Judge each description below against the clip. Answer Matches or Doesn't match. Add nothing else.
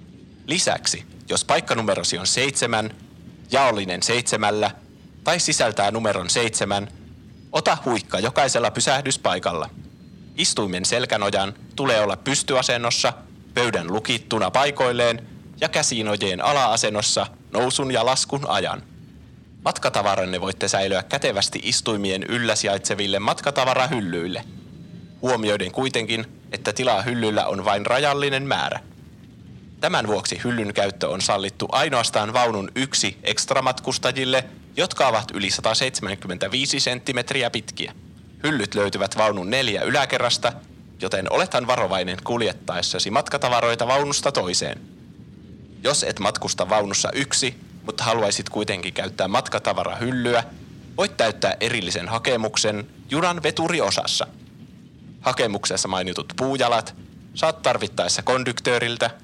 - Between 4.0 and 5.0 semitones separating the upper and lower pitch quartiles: Matches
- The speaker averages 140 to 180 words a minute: Doesn't match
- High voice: Doesn't match